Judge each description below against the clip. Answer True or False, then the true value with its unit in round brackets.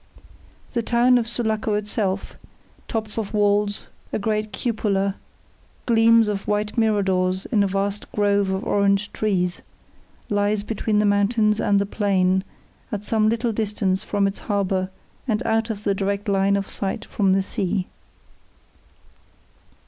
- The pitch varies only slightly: True (1.7 semitones)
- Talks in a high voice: True (205 Hz)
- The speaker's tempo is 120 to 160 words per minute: True (140 wpm)